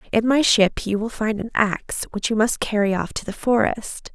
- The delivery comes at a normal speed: No, fast, 230 wpm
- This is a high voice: Yes, high, 220 Hz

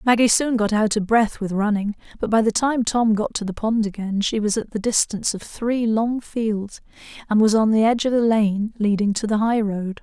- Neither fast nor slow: No, fast, 235 wpm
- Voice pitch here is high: Yes, high, 215 Hz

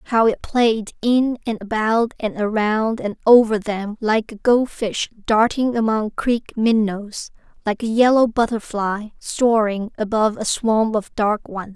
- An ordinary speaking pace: Yes, average, 150 wpm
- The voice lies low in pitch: No, high, 220 Hz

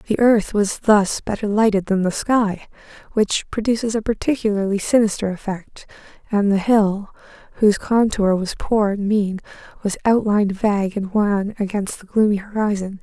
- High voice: Yes, high, 205 Hz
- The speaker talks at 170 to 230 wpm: No, average, 150 wpm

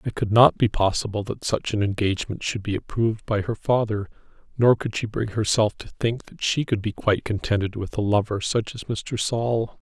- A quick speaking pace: Yes, fast, 215 wpm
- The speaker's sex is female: No, male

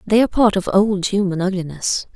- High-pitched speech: Yes, high, 195 Hz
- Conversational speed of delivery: Yes, average, 195 wpm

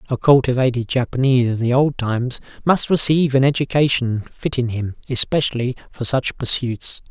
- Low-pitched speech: Yes, low, 130 Hz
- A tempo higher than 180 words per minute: No, average, 145 wpm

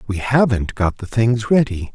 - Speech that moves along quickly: No, average, 185 wpm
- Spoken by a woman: No, male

